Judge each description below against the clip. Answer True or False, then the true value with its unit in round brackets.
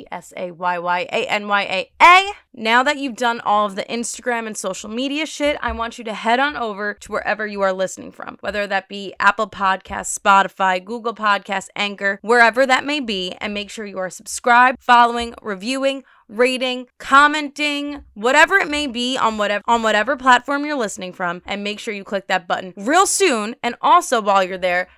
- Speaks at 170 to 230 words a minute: True (200 wpm)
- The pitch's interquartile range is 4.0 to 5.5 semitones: True (4.5 semitones)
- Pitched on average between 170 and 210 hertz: False (225 Hz)